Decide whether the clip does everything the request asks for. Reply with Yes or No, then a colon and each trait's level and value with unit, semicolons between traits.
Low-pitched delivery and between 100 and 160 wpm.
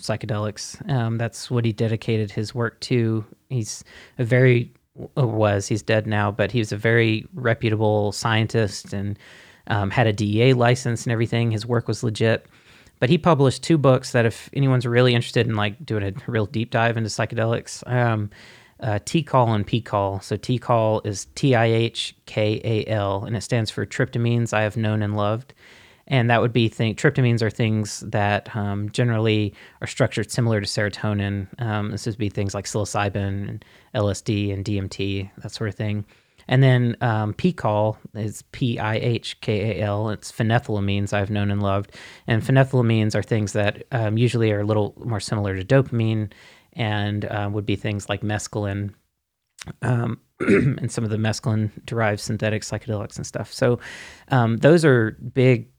No: low, 110 Hz; average, 170 wpm